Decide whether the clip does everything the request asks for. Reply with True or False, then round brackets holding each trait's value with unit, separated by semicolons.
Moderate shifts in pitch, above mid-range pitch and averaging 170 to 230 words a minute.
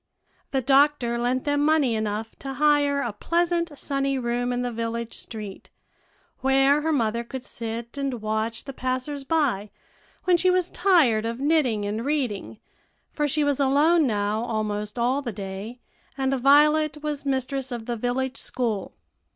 False (4.0 semitones; 260 Hz; 160 wpm)